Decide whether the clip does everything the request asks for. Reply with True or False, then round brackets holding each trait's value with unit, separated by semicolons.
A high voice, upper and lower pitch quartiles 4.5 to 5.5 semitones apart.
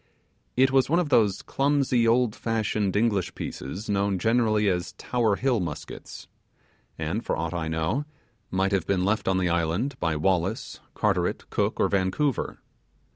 False (100 Hz; 4.8 semitones)